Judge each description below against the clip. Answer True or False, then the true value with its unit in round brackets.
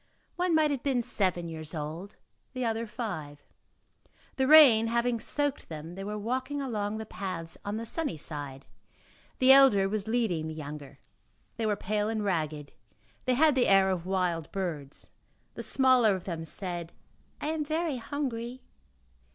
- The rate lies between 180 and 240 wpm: False (160 wpm)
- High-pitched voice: True (210 Hz)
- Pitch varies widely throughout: True (7.2 semitones)